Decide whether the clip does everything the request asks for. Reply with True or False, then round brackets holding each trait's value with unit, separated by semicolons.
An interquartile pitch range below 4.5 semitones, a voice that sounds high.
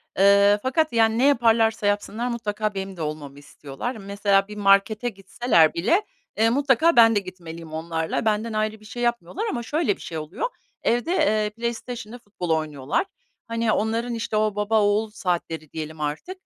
True (4.1 semitones; 215 Hz)